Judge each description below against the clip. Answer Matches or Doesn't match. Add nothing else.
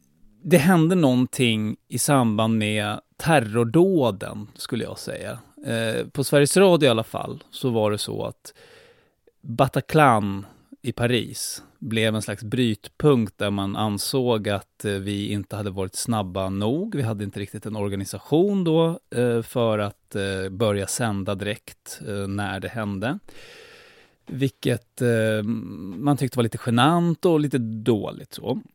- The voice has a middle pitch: Doesn't match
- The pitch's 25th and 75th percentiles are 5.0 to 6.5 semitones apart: Matches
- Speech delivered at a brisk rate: Doesn't match